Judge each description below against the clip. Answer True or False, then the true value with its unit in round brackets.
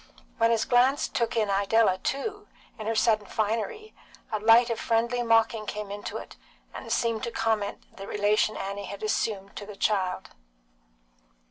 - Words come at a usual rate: True (160 wpm)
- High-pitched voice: True (220 Hz)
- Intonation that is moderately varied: False (2.1 semitones)